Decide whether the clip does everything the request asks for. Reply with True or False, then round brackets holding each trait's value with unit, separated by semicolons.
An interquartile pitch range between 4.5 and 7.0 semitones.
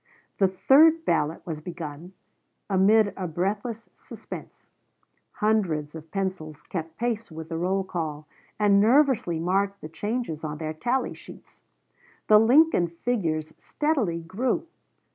True (5.6 semitones)